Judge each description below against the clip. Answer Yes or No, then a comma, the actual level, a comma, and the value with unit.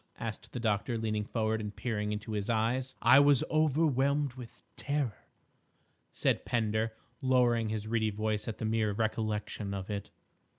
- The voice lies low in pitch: Yes, low, 110 Hz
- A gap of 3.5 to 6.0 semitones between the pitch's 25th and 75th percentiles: No, average, 2.9 semitones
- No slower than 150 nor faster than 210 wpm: Yes, average, 155 wpm